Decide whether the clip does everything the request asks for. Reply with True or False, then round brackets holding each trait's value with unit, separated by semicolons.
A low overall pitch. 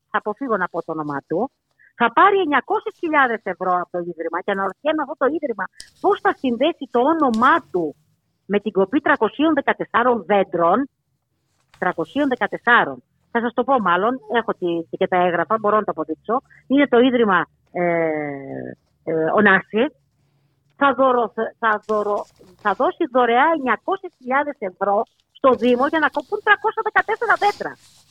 False (225 Hz)